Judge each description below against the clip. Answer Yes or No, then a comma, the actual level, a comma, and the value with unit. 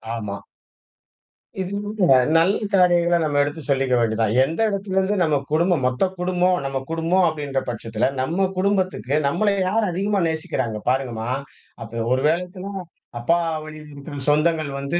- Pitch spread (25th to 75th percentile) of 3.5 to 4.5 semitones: No, wide, 5.5 semitones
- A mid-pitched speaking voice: Yes, medium, 160 Hz